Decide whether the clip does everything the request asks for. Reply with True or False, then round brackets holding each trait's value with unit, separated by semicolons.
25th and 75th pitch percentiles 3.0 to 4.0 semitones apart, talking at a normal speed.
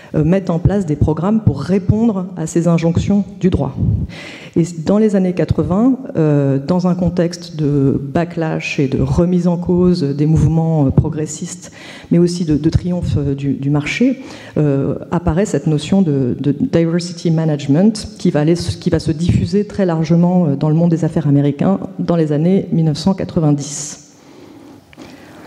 True (3.3 semitones; 155 wpm)